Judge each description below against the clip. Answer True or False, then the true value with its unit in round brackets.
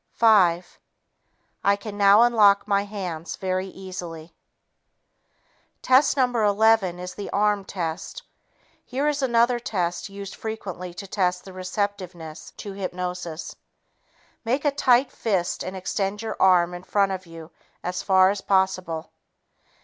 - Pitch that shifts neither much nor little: True (3.0 semitones)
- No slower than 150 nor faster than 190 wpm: False (135 wpm)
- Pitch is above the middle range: True (195 Hz)